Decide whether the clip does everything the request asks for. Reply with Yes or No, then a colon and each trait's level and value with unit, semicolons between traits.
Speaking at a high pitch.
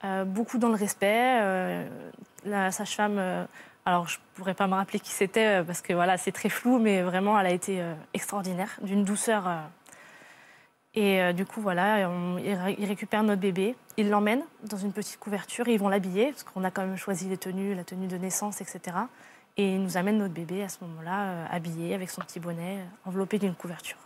Yes: high, 195 Hz